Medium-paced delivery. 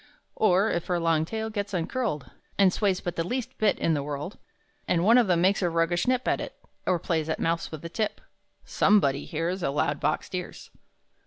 No: fast, 210 wpm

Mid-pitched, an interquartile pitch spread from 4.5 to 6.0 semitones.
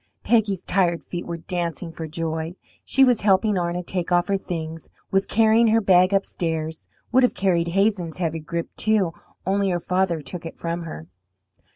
No: medium, 180 Hz; average, 2.9 semitones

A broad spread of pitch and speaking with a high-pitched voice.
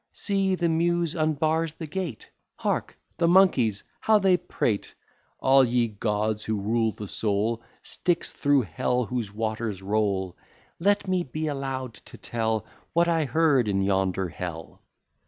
No: wide, 7.6 semitones; low, 125 Hz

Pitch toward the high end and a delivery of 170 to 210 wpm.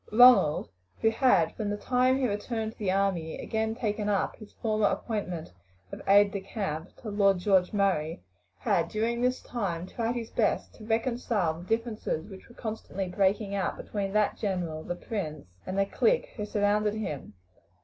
Yes: high, 205 Hz; average, 175 wpm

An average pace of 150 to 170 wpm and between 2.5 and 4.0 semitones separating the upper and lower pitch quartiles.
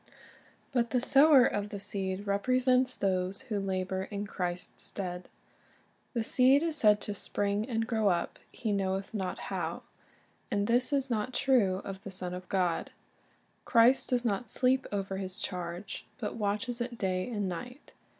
No: average, 160 wpm; average, 4.5 semitones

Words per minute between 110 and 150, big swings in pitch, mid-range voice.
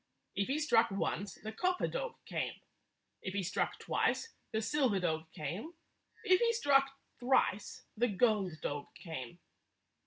No: average, 145 wpm; wide, 7.6 semitones; high, 220 Hz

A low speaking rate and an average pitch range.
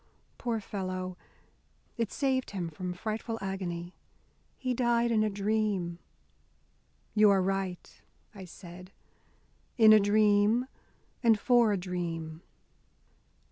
Yes: slow, 110 wpm; average, 3.4 semitones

